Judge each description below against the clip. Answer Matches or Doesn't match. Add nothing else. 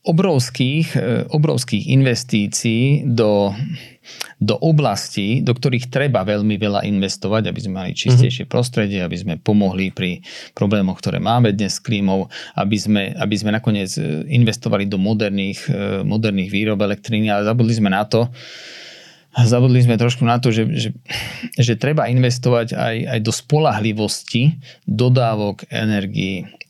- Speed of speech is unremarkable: Matches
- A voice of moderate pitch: Doesn't match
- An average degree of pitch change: Matches